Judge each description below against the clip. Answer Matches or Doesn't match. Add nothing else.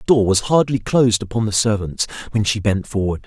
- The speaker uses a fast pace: Matches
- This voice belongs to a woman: Doesn't match